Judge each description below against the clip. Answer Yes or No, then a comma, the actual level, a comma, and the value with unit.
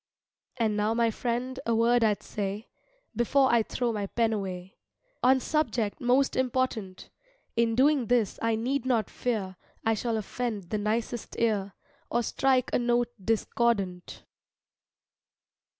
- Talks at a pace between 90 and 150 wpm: Yes, slow, 135 wpm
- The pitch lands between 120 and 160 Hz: No, high, 230 Hz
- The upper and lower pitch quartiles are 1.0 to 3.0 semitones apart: Yes, narrow, 2.6 semitones